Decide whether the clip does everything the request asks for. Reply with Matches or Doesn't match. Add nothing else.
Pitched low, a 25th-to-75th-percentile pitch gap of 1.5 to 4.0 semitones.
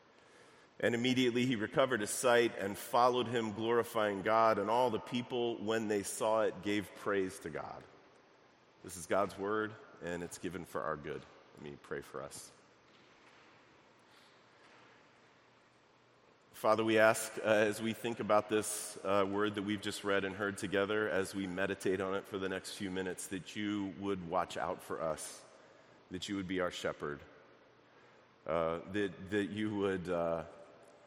Matches